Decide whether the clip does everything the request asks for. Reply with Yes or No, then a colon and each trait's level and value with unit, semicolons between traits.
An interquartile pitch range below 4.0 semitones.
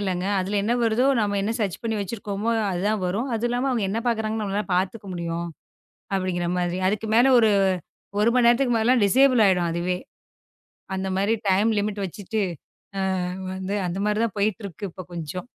Yes: average, 3.1 semitones